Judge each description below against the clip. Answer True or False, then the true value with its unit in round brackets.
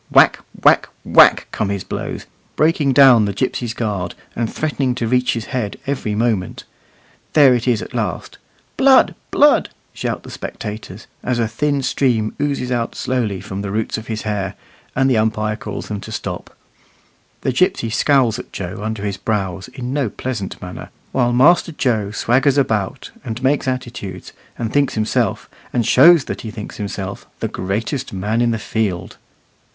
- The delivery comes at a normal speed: True (170 wpm)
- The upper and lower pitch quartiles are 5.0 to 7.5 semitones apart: False (3.8 semitones)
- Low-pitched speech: True (115 Hz)